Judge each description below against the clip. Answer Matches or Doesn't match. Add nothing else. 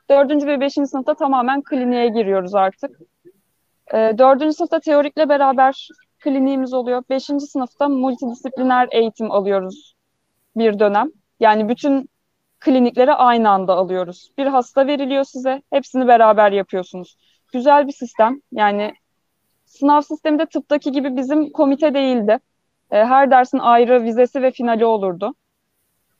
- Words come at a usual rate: Matches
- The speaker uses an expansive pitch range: Doesn't match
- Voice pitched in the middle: Doesn't match